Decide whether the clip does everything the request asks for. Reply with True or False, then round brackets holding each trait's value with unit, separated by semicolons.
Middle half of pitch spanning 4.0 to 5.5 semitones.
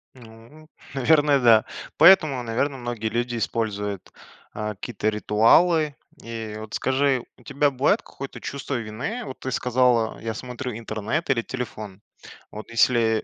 False (3.6 semitones)